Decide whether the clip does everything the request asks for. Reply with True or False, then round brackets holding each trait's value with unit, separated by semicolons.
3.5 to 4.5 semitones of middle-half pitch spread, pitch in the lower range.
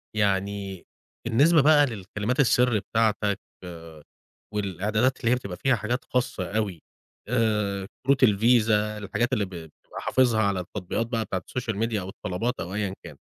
True (3.8 semitones; 105 Hz)